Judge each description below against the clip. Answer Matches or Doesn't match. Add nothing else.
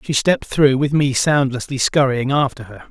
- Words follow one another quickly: Doesn't match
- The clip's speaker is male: Matches